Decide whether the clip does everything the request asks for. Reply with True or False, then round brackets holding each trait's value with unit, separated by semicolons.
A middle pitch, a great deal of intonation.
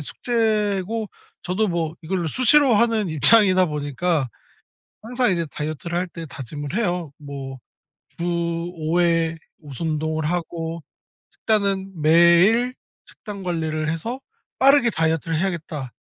False (170 Hz; 4.4 semitones)